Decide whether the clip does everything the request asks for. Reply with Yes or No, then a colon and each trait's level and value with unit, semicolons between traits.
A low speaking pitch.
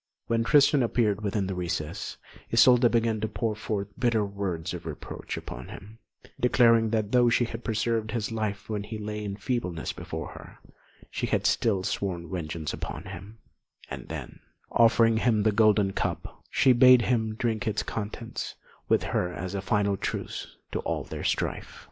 Yes: low, 110 Hz